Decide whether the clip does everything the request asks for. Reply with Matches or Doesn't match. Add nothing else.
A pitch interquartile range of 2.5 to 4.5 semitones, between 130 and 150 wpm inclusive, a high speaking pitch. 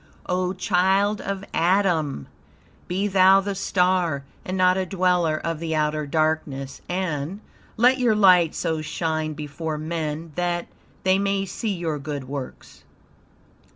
Doesn't match